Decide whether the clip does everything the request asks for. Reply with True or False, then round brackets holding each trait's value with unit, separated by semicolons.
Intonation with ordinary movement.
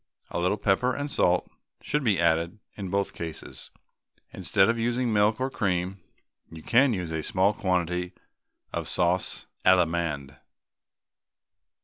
True (4.3 semitones)